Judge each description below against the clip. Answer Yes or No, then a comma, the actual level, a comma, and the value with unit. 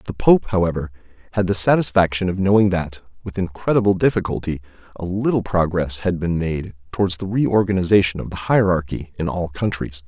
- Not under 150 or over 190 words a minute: Yes, average, 160 wpm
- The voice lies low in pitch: Yes, very low, 90 Hz